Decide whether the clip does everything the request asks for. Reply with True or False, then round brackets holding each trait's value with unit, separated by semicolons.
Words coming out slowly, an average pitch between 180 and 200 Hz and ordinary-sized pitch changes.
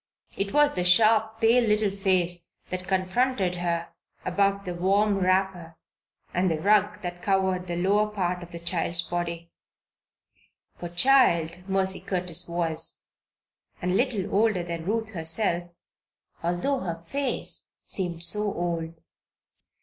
True (130 wpm; 185 Hz; 3.2 semitones)